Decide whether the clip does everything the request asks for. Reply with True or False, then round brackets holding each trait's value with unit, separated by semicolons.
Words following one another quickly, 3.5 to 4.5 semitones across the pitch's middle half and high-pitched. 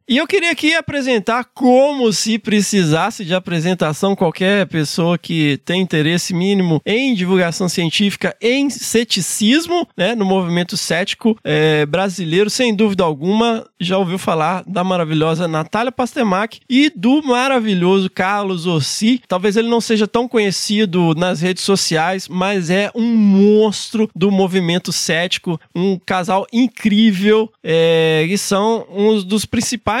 False (135 wpm; 4.1 semitones; 195 Hz)